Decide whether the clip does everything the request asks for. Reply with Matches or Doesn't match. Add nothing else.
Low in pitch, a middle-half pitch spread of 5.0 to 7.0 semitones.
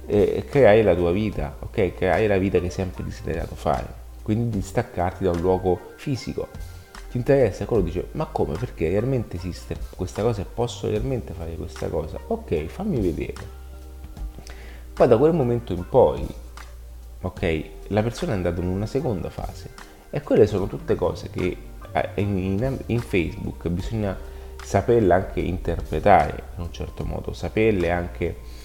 Matches